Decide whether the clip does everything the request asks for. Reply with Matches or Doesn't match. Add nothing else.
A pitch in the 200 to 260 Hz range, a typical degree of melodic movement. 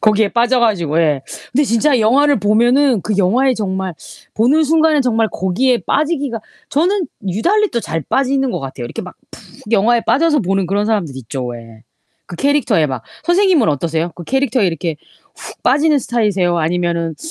Doesn't match